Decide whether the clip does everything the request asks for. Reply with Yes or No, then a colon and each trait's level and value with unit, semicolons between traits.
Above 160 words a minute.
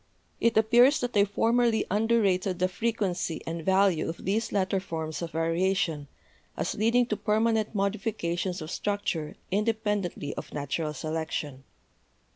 No: average, 140 wpm